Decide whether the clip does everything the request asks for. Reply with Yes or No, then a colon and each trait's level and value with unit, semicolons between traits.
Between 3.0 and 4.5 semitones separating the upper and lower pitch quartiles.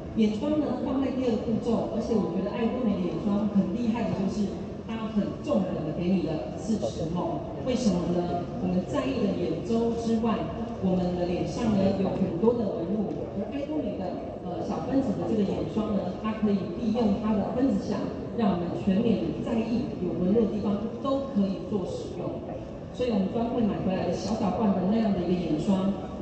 Yes: average, 3.4 semitones